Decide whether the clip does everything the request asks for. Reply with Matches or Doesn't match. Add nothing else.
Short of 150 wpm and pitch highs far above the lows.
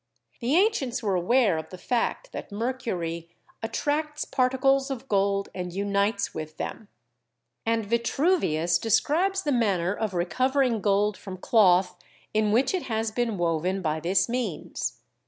Matches